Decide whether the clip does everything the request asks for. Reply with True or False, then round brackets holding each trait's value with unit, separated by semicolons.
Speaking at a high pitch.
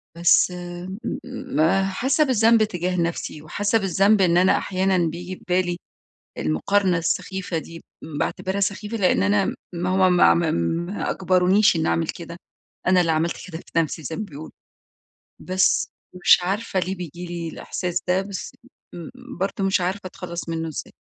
False (180 Hz)